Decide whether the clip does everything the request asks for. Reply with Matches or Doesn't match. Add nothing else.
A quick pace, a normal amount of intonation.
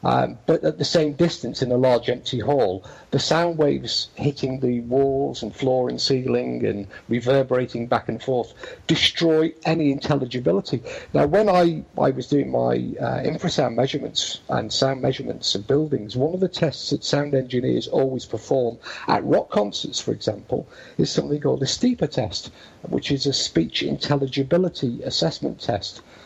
Doesn't match